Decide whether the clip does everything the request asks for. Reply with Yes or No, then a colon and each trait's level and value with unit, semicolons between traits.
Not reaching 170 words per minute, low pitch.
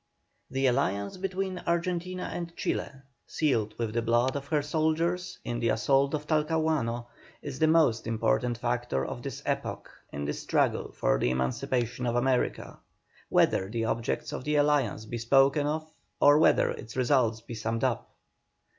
Yes: average, 160 wpm; low, 130 Hz